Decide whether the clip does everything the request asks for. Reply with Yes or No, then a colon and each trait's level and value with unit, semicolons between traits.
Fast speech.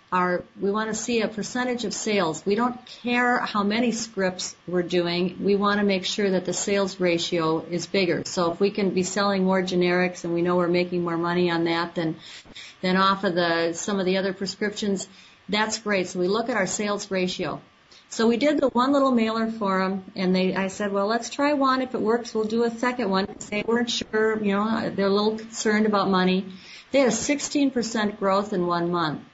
Yes: fast, 220 wpm